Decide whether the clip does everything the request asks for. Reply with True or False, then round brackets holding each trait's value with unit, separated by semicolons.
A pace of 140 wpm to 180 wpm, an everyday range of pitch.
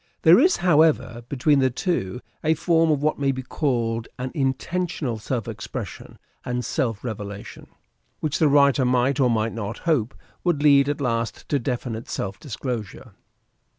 True (160 wpm; 4.2 semitones)